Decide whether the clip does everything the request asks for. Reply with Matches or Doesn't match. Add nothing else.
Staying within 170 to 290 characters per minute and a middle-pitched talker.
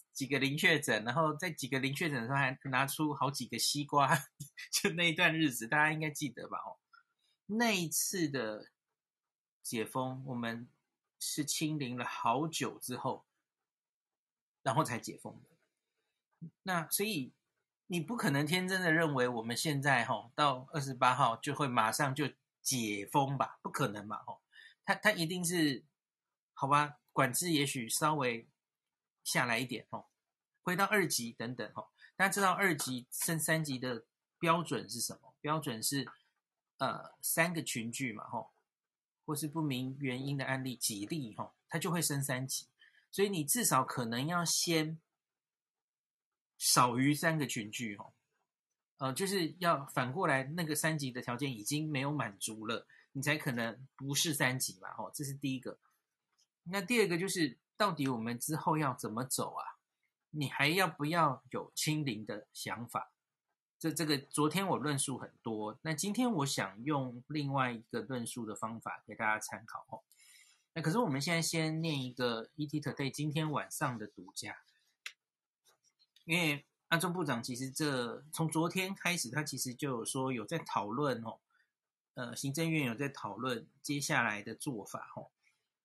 Matches